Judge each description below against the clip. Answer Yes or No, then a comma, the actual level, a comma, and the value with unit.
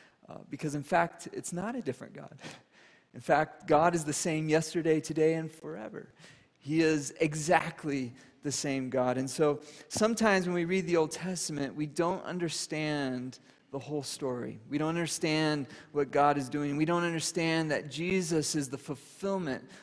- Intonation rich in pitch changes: No, average, 2.9 semitones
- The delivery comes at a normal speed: Yes, average, 165 wpm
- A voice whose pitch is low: No, medium, 155 Hz